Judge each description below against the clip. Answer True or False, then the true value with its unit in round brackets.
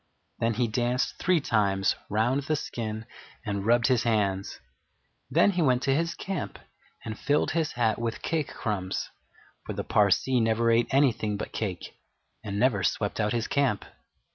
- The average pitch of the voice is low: True (115 Hz)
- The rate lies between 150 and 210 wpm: True (165 wpm)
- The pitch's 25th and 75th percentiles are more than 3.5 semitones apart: True (4.0 semitones)